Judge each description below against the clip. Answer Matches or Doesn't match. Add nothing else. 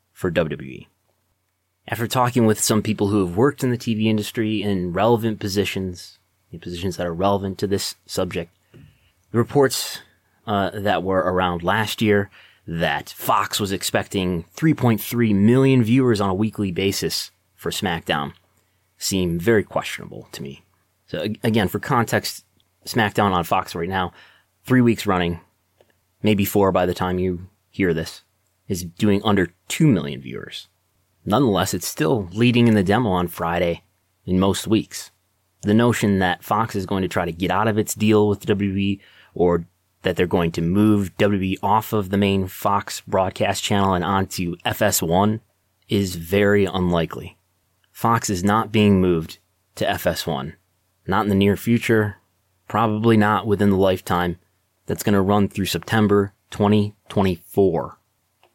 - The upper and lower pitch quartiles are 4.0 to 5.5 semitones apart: Doesn't match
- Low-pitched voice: Matches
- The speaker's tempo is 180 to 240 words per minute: Doesn't match